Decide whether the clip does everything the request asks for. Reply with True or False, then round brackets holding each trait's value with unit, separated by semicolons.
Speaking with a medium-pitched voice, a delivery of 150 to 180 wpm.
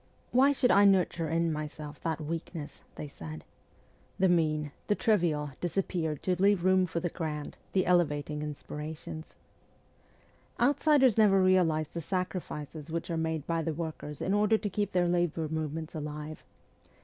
True (165 Hz; 160 wpm)